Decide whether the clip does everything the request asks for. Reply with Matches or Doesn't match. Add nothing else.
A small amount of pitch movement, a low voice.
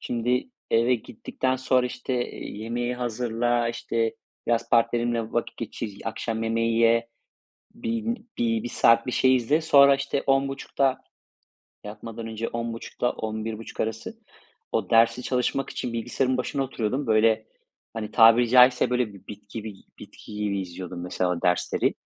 Matches